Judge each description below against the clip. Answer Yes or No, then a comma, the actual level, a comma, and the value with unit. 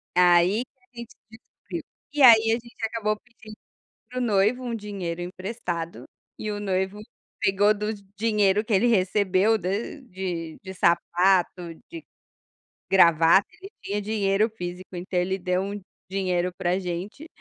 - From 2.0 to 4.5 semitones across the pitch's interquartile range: Yes, average, 3.3 semitones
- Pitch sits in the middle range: No, high, 195 Hz